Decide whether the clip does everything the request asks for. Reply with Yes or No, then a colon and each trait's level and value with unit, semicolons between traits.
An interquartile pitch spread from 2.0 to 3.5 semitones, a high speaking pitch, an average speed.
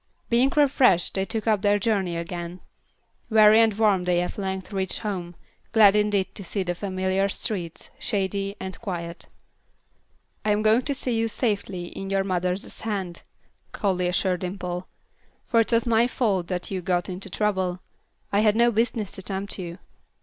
Yes: average, 2.9 semitones; high, 195 Hz; average, 170 wpm